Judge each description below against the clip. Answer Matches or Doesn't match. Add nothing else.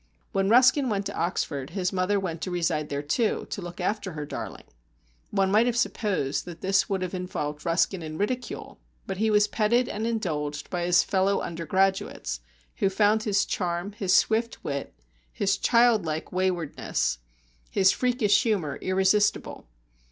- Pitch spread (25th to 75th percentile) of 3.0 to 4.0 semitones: Matches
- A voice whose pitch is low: Doesn't match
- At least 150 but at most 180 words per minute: Matches